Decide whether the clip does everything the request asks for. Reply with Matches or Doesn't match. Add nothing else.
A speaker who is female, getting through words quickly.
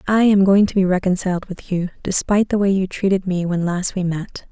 Matches